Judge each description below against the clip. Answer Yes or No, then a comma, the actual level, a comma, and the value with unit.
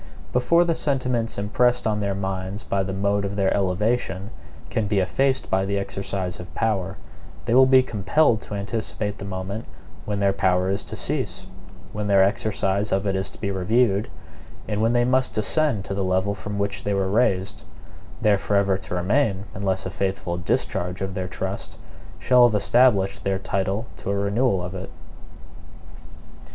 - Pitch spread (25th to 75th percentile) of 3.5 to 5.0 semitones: No, average, 2.7 semitones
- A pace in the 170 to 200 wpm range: Yes, average, 175 wpm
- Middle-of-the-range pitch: No, low, 100 Hz